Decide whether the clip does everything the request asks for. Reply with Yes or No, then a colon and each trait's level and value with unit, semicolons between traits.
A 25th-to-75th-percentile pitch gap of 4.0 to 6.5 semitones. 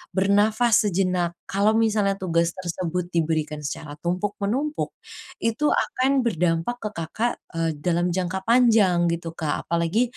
Yes: average, 4.5 semitones